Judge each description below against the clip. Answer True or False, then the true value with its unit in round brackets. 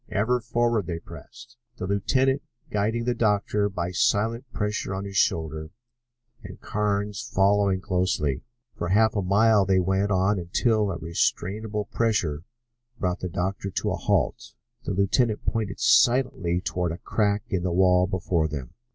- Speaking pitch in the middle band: False (100 Hz)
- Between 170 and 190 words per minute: False (150 wpm)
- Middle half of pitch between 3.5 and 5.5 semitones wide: False (3.1 semitones)